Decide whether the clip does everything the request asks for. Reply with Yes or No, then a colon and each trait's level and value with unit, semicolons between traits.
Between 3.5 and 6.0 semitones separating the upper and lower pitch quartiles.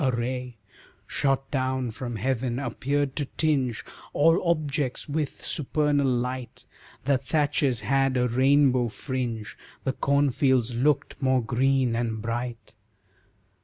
No: narrow, 2.6 semitones